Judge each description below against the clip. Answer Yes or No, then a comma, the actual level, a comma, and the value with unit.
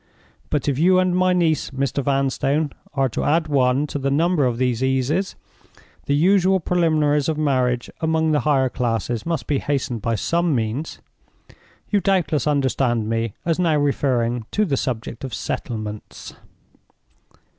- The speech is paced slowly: No, average, 155 wpm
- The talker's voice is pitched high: No, medium, 140 Hz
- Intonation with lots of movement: No, average, 4.4 semitones